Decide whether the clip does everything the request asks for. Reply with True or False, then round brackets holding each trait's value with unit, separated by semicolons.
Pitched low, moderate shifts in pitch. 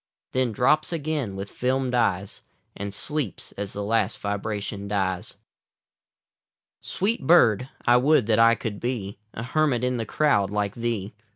True (115 Hz; 4.2 semitones)